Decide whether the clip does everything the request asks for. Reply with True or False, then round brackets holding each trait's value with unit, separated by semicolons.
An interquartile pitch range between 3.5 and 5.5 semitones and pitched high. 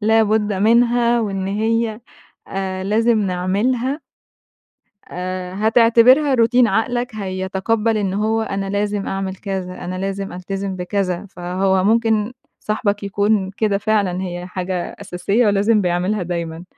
False (3.0 semitones; 200 Hz)